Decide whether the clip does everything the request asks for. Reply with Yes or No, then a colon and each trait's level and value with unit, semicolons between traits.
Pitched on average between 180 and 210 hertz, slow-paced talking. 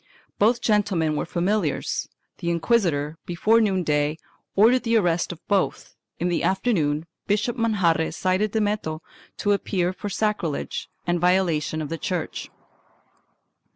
Yes: medium, 185 Hz; slow, 130 wpm